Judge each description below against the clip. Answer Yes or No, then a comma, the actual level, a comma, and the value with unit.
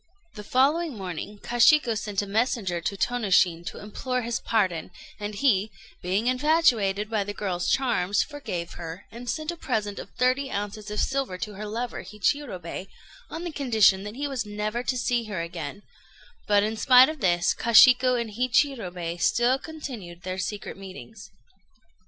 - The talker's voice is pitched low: No, high, 215 Hz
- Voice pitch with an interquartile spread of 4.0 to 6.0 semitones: Yes, average, 4.6 semitones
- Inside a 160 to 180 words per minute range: Yes, average, 165 wpm